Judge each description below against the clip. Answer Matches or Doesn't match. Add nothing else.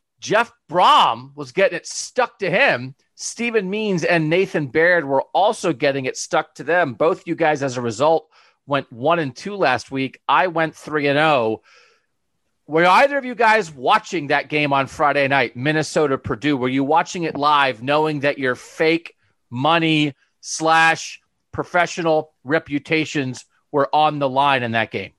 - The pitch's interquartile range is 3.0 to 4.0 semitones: Matches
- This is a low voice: Doesn't match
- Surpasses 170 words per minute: Doesn't match